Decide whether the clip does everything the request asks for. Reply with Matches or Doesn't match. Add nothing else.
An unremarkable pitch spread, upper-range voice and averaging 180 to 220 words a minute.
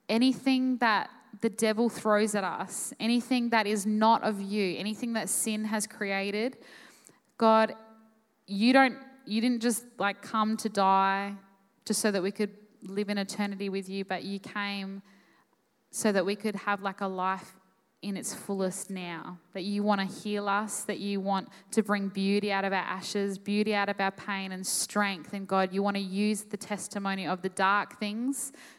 Doesn't match